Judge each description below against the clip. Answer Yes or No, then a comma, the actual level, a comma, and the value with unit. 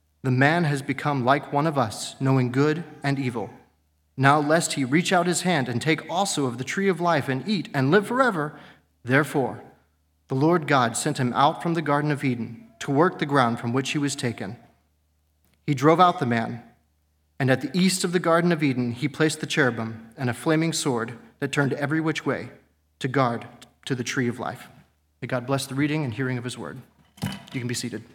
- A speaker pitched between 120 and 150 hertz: Yes, low, 135 Hz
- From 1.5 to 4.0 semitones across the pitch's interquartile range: No, average, 4.7 semitones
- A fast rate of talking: Yes, fast, 215 wpm